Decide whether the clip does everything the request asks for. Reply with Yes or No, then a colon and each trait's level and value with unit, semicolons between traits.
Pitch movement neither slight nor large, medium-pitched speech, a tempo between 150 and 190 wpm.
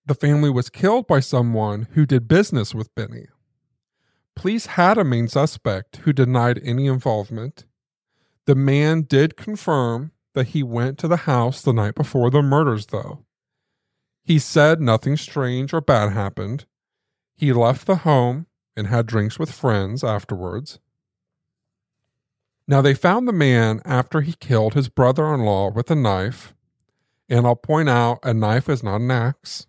No: average, 4.2 semitones; low, 130 Hz; average, 160 wpm